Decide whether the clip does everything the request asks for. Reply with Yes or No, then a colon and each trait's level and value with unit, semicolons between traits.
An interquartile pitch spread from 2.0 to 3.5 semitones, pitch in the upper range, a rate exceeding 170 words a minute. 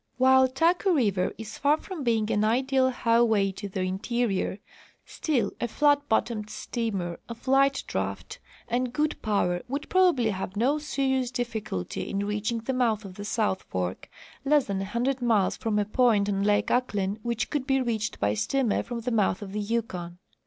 No: average, 4.2 semitones; high, 230 Hz; average, 180 wpm